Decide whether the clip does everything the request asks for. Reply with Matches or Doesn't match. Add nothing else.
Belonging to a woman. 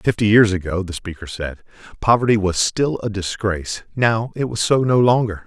Doesn't match